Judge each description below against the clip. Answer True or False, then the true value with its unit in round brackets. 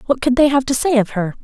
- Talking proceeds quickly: True (335 wpm)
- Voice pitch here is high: True (250 Hz)